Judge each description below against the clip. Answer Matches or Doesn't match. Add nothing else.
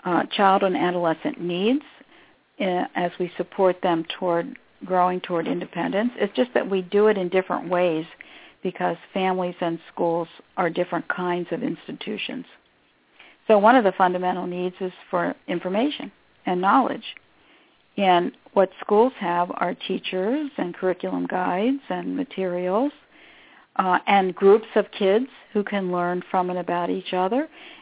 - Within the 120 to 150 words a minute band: Matches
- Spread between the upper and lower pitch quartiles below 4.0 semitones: Matches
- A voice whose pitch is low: Doesn't match